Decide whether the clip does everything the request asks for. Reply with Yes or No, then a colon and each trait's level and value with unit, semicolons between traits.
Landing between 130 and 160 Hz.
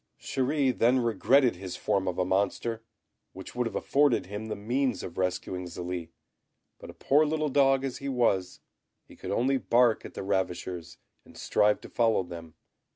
No: low, 110 Hz